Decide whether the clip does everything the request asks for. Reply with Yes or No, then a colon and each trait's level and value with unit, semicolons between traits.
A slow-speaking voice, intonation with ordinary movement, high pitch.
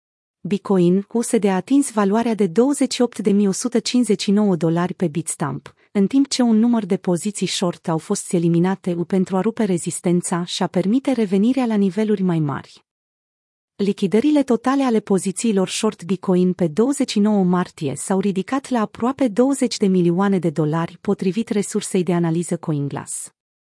No: average, 140 wpm; average, 4.2 semitones; high, 200 Hz